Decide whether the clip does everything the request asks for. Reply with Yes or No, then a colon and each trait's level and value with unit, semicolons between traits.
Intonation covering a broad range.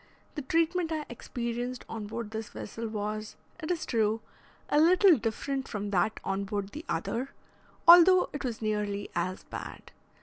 Yes: wide, 6.3 semitones